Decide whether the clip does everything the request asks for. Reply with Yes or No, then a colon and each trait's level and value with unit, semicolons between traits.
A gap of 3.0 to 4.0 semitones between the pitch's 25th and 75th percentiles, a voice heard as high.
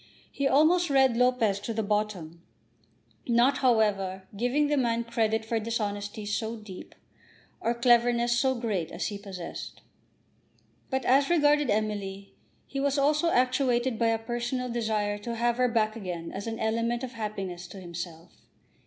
Yes: average, 3.5 semitones; high, 230 Hz